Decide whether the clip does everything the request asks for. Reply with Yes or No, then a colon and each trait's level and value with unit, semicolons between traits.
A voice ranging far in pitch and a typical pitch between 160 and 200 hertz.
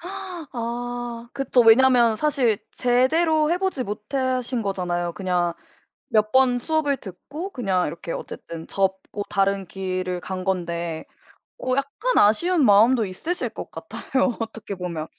No: wide, 6.1 semitones; high, 230 Hz